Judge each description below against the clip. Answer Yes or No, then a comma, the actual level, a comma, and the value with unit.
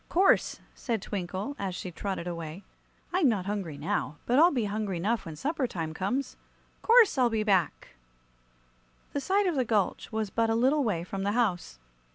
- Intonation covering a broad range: Yes, wide, 6.1 semitones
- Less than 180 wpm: No, average, 185 wpm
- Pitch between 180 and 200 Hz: No, high, 215 Hz